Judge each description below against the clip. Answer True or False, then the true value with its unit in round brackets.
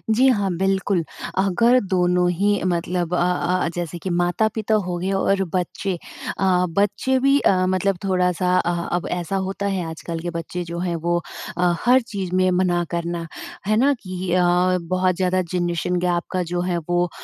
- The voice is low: False (180 Hz)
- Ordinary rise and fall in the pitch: False (1.9 semitones)